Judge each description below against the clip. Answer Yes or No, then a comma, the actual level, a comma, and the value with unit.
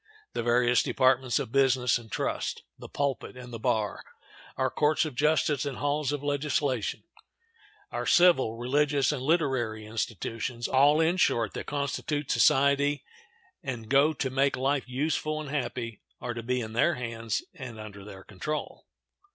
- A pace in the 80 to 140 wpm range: No, average, 155 wpm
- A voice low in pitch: Yes, low, 130 Hz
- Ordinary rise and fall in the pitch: Yes, average, 3.5 semitones